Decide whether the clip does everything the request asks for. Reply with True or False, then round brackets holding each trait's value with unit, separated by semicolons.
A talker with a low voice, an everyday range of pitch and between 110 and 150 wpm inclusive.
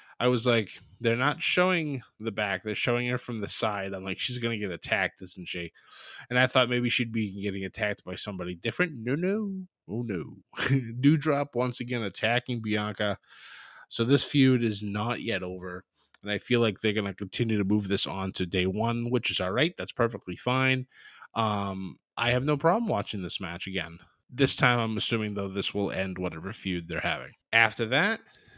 False (110 Hz; 4.3 semitones; 200 wpm)